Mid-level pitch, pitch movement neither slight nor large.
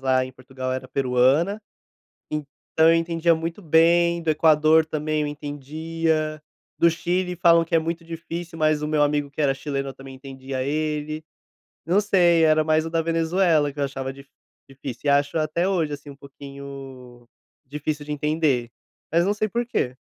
Yes: medium, 155 Hz; average, 3.1 semitones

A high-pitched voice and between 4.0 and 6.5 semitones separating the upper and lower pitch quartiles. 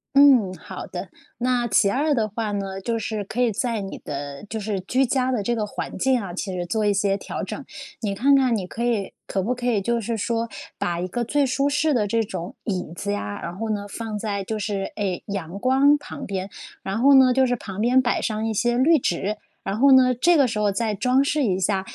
Yes: high, 220 Hz; average, 4.3 semitones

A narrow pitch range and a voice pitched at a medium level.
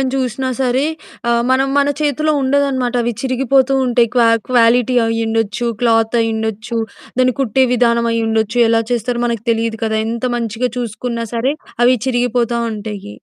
No: narrow, 2.0 semitones; high, 235 Hz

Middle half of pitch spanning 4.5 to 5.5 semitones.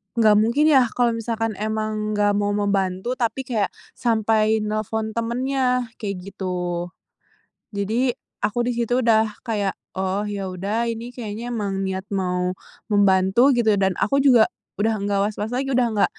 No: average, 2.9 semitones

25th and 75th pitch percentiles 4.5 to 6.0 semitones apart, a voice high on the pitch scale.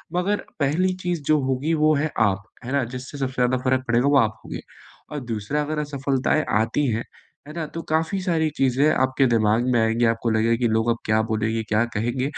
No: average, 4.9 semitones; low, 130 Hz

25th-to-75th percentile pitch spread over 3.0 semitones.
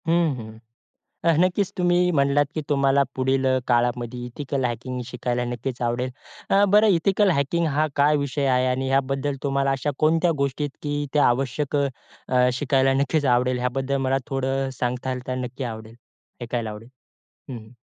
No: average, 2.7 semitones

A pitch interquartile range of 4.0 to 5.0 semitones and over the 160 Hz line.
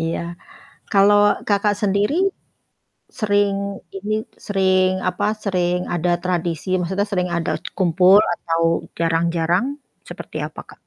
No: average, 2.8 semitones; medium, 185 Hz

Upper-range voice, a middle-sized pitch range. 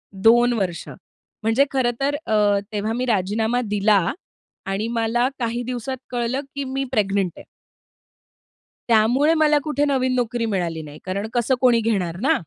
Yes: high, 230 Hz; average, 3.8 semitones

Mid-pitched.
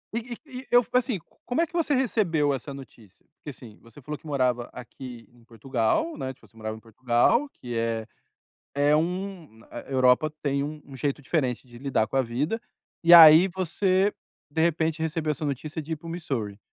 Yes: medium, 145 Hz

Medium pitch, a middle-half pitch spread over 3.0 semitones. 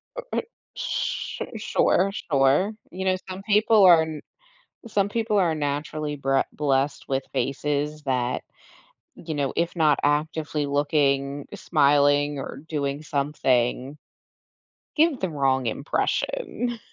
Yes: medium, 150 Hz; average, 4.1 semitones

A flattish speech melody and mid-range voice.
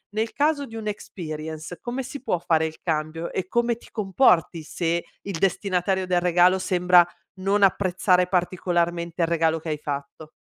No: average, 3.0 semitones; medium, 180 Hz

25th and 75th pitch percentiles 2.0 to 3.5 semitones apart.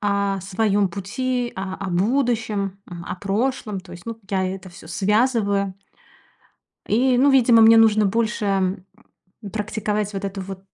Yes: average, 2.9 semitones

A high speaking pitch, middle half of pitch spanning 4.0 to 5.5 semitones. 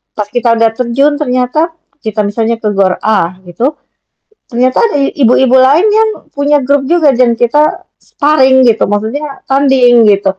Yes: very high, 250 Hz; average, 4.3 semitones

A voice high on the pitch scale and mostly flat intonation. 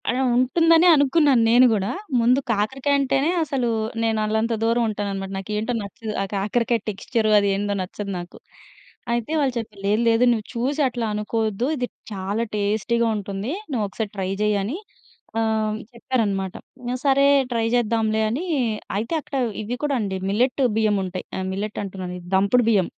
No: high, 220 Hz; average, 3.5 semitones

